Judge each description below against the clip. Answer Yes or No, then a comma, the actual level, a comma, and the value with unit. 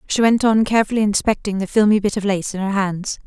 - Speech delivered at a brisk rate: Yes, fast, 240 wpm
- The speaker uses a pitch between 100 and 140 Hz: No, high, 205 Hz